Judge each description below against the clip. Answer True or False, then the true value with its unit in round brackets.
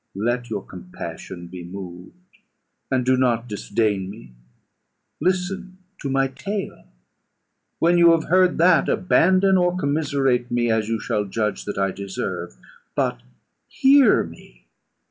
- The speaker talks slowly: True (130 wpm)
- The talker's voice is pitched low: True (125 Hz)